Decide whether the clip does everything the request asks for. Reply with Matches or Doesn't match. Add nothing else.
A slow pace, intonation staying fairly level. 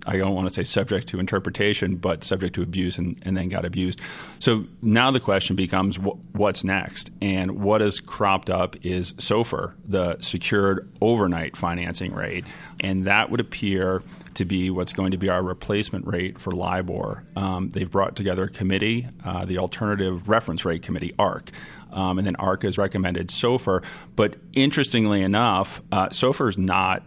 Doesn't match